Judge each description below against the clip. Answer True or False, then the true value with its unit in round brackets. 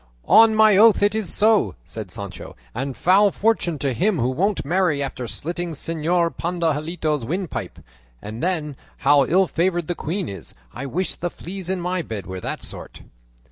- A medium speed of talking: True (175 wpm)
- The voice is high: False (170 Hz)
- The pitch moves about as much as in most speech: True (4.9 semitones)